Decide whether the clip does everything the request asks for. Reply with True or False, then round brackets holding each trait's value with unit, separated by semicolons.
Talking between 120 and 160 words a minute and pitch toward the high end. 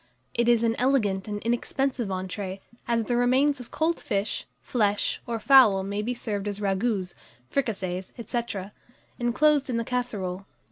True (150 wpm; 230 Hz)